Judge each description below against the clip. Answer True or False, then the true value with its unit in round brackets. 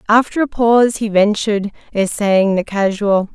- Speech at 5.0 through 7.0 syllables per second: False (4.8 syllables/s)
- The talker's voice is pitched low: False (210 Hz)